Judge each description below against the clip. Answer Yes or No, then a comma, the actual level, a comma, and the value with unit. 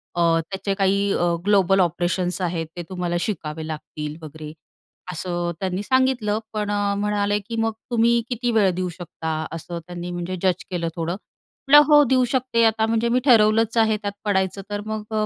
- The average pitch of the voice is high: Yes, high, 200 Hz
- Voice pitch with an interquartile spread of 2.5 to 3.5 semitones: No, average, 4.0 semitones